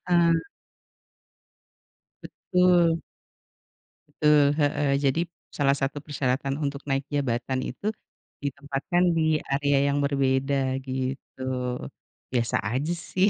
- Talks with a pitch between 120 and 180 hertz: Yes, medium, 140 Hz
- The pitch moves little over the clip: Yes, narrow, 2.3 semitones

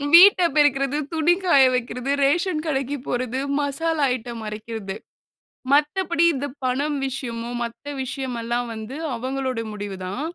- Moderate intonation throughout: Yes, average, 3.7 semitones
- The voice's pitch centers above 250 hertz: Yes, very high, 265 Hz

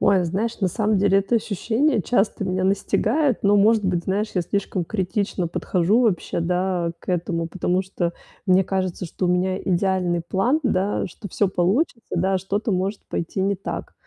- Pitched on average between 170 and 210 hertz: Yes, high, 190 Hz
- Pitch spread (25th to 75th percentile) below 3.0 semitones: Yes, narrow, 2.4 semitones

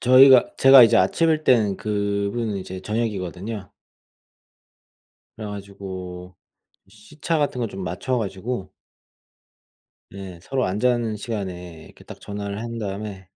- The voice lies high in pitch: No, low, 105 Hz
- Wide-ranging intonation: No, average, 3.9 semitones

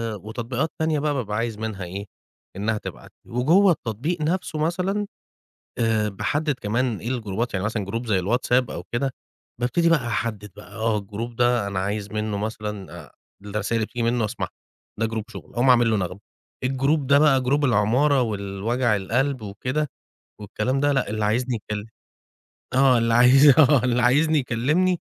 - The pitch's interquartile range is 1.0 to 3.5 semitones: No, average, 4.2 semitones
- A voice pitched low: Yes, low, 120 Hz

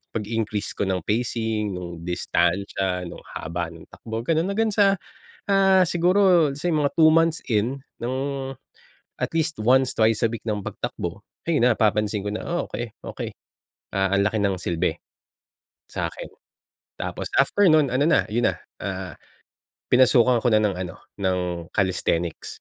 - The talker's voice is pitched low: Yes, low, 110 Hz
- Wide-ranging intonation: Yes, wide, 7.4 semitones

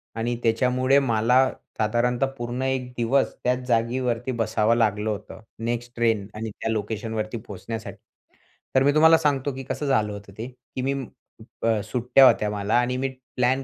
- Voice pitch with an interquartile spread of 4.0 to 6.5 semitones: No, average, 2.8 semitones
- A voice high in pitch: No, low, 120 Hz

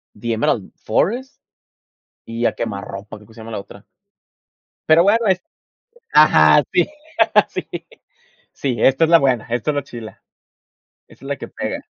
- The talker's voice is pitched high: No, low, 120 Hz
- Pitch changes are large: Yes, wide, 6.5 semitones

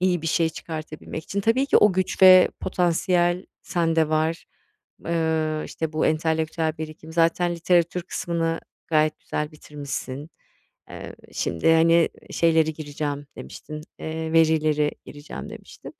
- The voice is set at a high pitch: No, medium, 160 Hz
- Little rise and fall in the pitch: Yes, narrow, 1.5 semitones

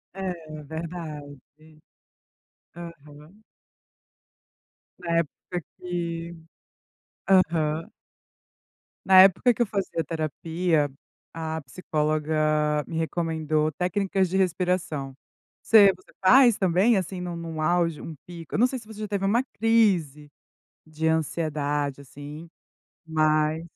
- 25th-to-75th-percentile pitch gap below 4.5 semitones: Yes, average, 3.4 semitones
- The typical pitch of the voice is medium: Yes, medium, 165 Hz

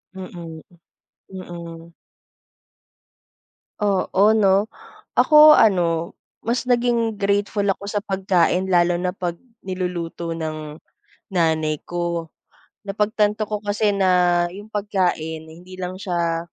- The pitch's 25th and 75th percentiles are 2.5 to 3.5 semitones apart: Yes, average, 3.2 semitones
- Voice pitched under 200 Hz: Yes, medium, 185 Hz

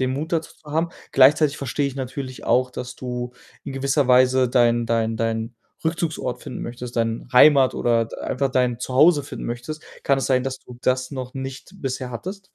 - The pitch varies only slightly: Yes, narrow, 2.1 semitones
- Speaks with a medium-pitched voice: No, low, 130 Hz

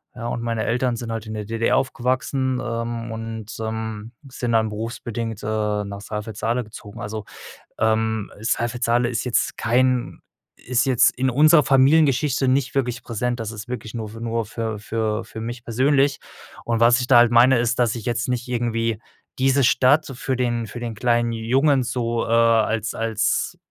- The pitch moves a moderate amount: No, narrow, 1.9 semitones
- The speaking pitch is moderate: No, low, 115 Hz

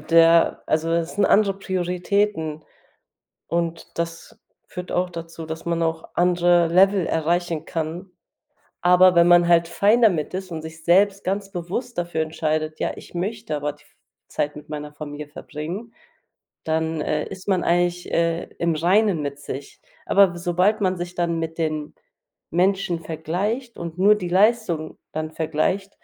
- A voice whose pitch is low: No, medium, 170 Hz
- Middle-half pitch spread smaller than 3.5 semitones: Yes, average, 2.7 semitones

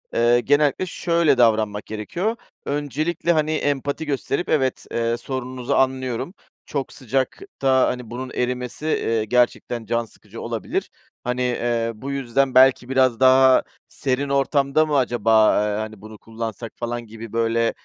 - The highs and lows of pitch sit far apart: No, average, 3.1 semitones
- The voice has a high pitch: No, low, 125 Hz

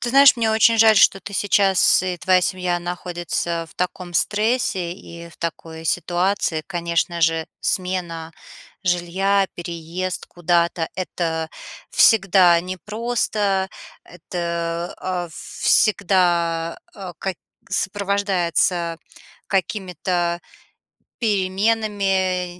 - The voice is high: No, medium, 180 Hz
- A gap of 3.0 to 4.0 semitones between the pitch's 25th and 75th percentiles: No, narrow, 2.4 semitones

